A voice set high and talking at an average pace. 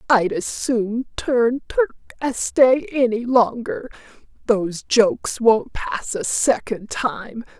No: high, 235 Hz; slow, 125 wpm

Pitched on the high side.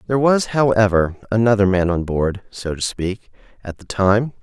No: low, 105 Hz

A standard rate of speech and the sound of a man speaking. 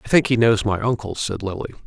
No: fast, 255 wpm; male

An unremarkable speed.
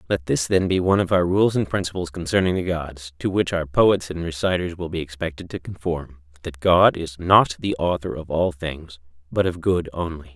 No: fast, 210 wpm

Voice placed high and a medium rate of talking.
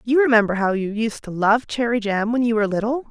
No: high, 225 Hz; fast, 250 wpm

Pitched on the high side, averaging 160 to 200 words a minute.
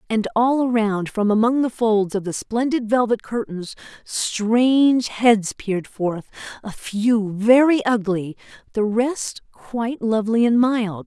No: high, 225 Hz; average, 140 wpm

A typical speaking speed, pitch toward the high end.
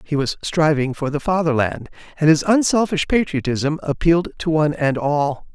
No: average, 160 wpm; medium, 155 Hz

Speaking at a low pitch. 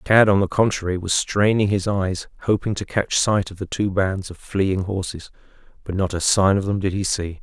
Yes: very low, 95 Hz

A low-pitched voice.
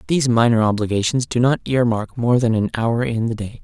Yes: low, 115 Hz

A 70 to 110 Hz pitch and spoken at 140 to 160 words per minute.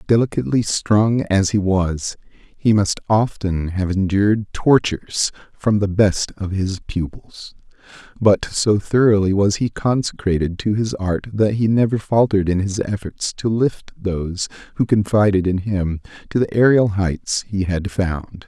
Yes: low, 100 Hz; average, 155 wpm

